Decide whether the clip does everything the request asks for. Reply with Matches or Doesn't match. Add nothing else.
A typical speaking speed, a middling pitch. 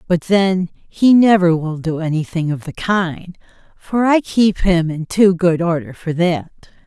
Matches